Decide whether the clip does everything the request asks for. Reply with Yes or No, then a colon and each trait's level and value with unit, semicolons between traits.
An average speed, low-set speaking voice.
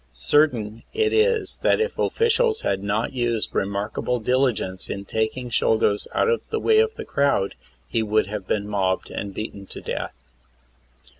Yes: average, 170 wpm; low, 115 Hz